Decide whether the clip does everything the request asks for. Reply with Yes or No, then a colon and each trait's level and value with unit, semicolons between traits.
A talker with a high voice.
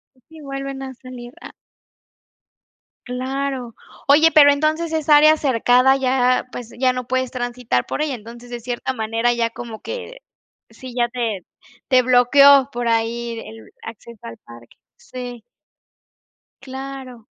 Yes: very high, 250 Hz